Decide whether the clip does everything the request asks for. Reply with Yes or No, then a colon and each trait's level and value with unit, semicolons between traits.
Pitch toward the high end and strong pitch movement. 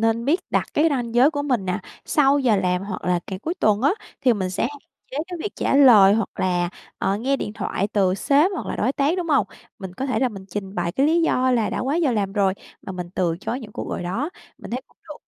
Yes: high, 230 Hz; wide, 6.4 semitones